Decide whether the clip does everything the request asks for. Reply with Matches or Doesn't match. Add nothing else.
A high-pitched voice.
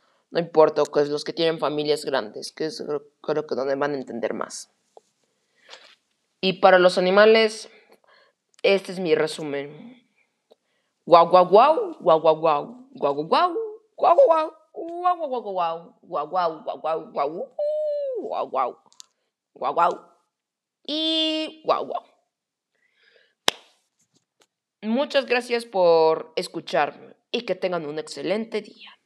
Matches